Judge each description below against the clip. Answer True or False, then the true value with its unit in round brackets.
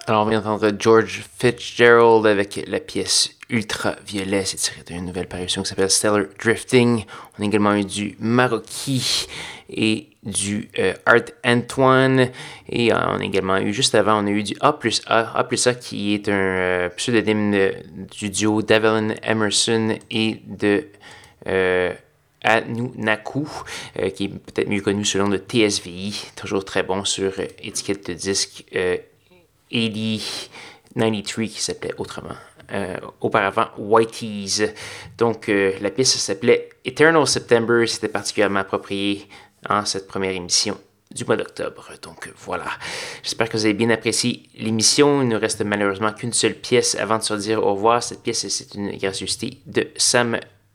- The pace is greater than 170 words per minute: False (160 wpm)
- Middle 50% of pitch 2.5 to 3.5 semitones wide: True (2.9 semitones)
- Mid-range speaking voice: False (110 Hz)